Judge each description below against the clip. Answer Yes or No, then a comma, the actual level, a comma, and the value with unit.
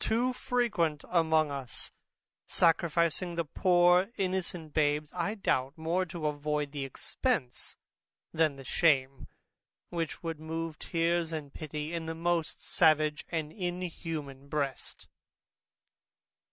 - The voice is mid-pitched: Yes, medium, 160 Hz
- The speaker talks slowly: Yes, slow, 115 wpm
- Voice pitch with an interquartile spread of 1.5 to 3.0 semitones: Yes, narrow, 2.6 semitones